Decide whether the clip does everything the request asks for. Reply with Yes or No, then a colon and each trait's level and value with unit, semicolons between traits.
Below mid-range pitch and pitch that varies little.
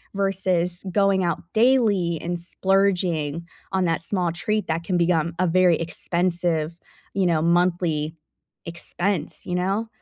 No: medium, 175 Hz; narrow, 2.3 semitones